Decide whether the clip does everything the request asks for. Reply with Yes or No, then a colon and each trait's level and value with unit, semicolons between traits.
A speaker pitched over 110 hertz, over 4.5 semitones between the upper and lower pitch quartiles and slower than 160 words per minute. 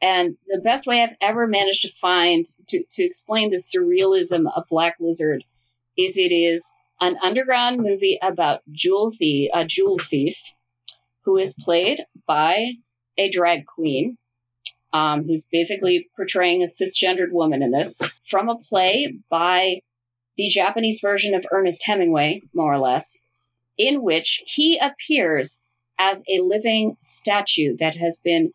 Yes: medium, 185 Hz; average, 4.9 semitones; average, 145 wpm